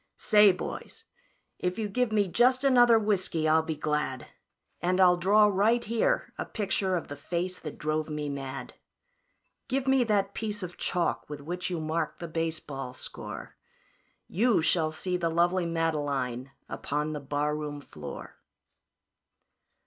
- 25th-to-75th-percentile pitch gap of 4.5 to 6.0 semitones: Yes, average, 5.3 semitones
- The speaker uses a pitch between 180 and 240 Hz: No, medium, 170 Hz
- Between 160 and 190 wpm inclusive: No, average, 150 wpm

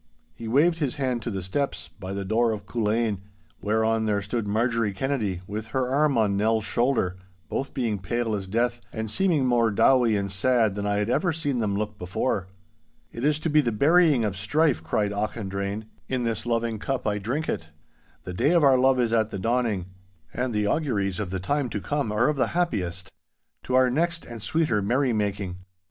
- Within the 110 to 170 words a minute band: No, average, 200 wpm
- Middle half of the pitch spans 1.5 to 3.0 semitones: No, average, 4.2 semitones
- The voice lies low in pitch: Yes, low, 115 Hz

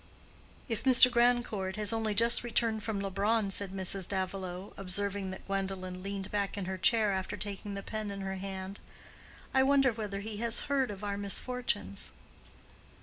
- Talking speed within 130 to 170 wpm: Yes, average, 160 wpm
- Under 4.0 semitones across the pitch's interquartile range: Yes, average, 2.8 semitones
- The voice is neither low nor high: No, high, 200 Hz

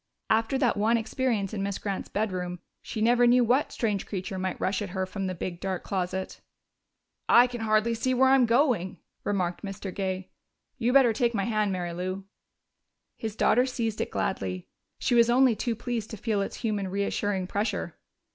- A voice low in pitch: No, high, 210 Hz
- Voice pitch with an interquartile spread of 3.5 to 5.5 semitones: Yes, average, 3.9 semitones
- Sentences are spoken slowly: No, average, 185 wpm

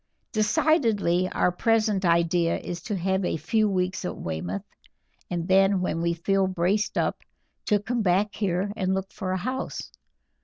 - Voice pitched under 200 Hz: Yes, high, 190 Hz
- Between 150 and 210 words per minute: Yes, average, 160 wpm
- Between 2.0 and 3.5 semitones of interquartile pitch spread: Yes, average, 2.9 semitones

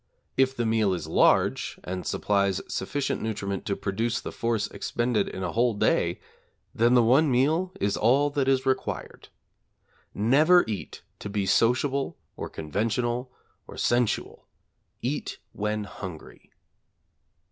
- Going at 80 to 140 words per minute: Yes, slow, 135 wpm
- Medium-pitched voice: No, low, 115 Hz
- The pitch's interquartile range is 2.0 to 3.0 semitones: No, average, 4.3 semitones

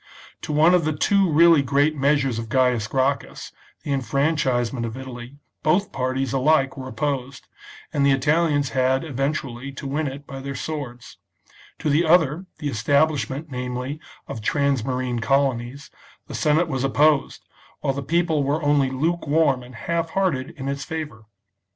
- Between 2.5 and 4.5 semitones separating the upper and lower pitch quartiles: Yes, average, 2.9 semitones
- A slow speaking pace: No, average, 155 wpm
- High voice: No, medium, 140 Hz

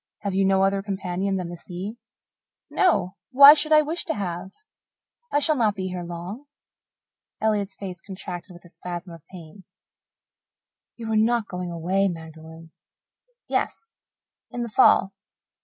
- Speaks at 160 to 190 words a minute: No, average, 150 wpm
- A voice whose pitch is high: Yes, high, 195 Hz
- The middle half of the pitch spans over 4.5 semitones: No, average, 3.7 semitones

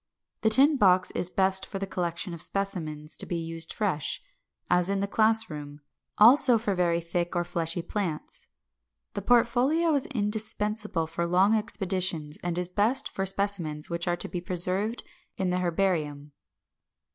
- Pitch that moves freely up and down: No, average, 3.8 semitones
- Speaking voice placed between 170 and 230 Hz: Yes, medium, 185 Hz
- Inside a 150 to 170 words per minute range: Yes, average, 160 wpm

